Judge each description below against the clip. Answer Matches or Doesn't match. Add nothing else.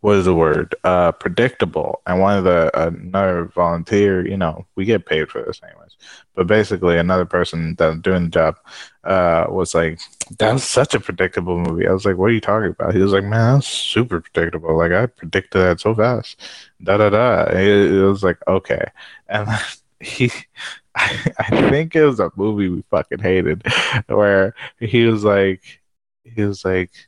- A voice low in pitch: Matches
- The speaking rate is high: Doesn't match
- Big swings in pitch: Doesn't match